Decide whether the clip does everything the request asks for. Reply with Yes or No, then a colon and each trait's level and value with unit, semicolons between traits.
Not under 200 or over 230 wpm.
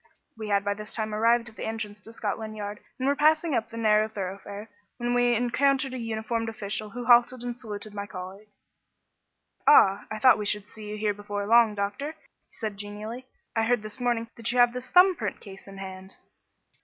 Yes: fast, 205 wpm